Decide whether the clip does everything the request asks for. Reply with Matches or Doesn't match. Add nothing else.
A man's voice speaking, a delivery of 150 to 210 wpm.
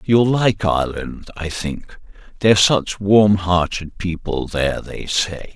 Doesn't match